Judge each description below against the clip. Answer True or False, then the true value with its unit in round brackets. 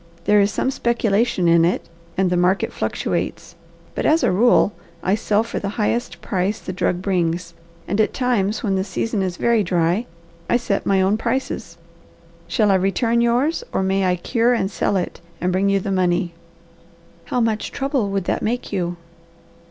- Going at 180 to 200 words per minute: True (185 wpm)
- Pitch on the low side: False (200 Hz)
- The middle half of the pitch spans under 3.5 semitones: False (4.0 semitones)